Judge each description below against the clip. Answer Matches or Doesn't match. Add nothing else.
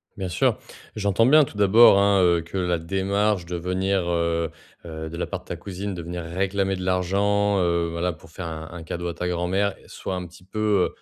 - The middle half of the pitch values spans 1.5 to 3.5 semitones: Matches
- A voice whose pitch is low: Matches